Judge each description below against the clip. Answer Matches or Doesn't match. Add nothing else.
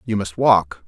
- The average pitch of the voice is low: Matches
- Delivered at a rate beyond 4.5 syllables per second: Doesn't match